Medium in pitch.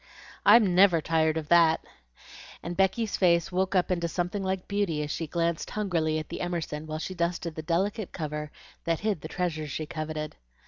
Yes: medium, 170 Hz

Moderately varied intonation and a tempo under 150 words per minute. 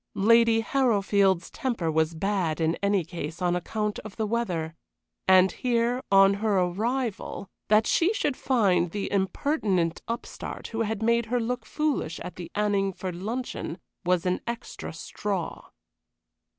Yes: average, 4.4 semitones; average, 140 wpm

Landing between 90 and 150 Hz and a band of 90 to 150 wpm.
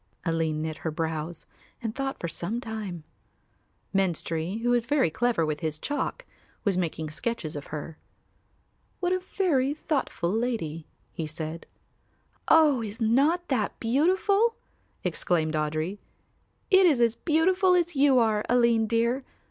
No: high, 225 Hz; average, 140 wpm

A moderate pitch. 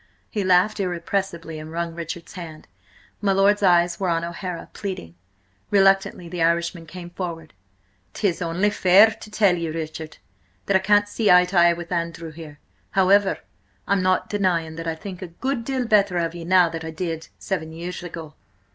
Yes: medium, 175 Hz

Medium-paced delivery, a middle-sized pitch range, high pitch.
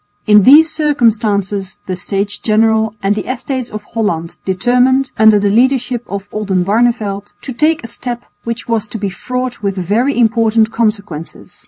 Yes: average, 155 wpm; average, 3.2 semitones; high, 220 Hz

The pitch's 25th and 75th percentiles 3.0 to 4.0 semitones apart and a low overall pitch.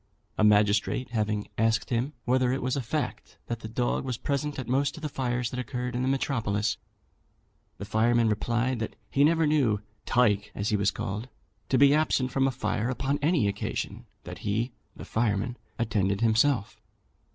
Yes: average, 3.6 semitones; low, 120 Hz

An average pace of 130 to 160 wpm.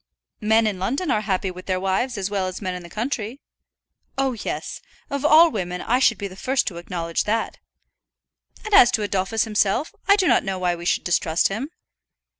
No: fast, 205 wpm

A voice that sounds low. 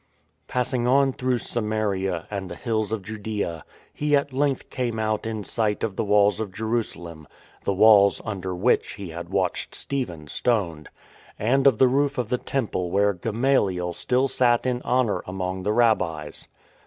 Yes: low, 110 Hz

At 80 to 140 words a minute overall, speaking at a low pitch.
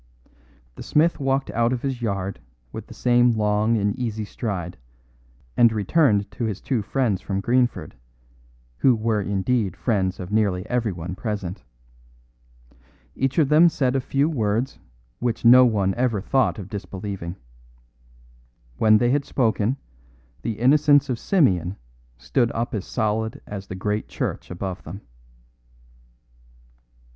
Yes: slow, 135 wpm; low, 110 Hz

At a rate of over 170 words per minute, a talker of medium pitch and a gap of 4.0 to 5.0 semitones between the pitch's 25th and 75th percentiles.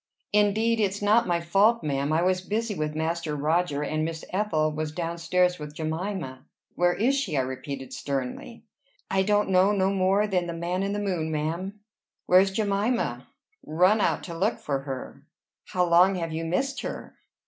Yes: average, 180 wpm; medium, 180 Hz; average, 4.4 semitones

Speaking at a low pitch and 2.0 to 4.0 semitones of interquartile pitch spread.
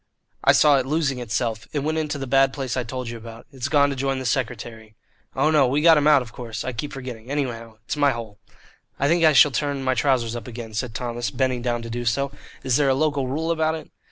Yes: low, 130 Hz; average, 3.3 semitones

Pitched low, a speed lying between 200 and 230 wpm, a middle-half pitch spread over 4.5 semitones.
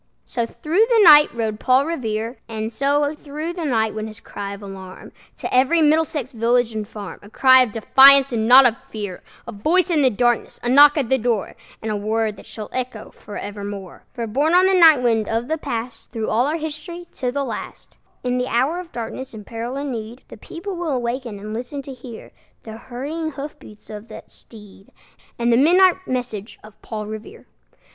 No: high, 245 Hz; fast, 205 wpm; average, 4.9 semitones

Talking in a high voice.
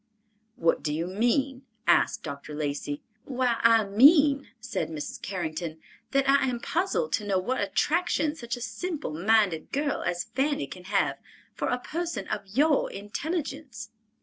Yes: high, 230 Hz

